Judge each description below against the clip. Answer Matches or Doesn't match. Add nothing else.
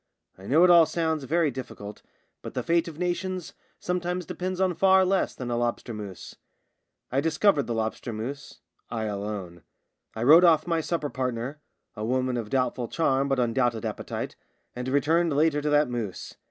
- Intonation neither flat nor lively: Doesn't match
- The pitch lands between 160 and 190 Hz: Doesn't match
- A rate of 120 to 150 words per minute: Doesn't match